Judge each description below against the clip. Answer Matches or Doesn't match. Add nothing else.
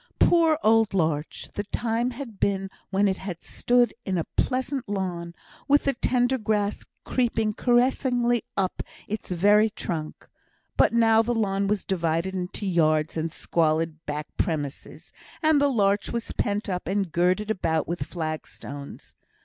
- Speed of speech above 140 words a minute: Matches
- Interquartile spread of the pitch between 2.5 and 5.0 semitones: Doesn't match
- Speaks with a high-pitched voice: Matches